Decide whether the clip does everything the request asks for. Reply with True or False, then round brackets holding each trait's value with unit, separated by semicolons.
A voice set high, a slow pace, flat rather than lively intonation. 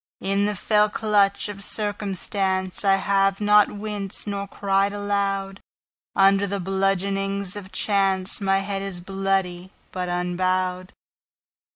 True (195 Hz; 105 wpm; 1.0 semitones)